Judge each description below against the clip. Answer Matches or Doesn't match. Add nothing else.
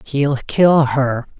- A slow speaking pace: Matches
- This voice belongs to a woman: Doesn't match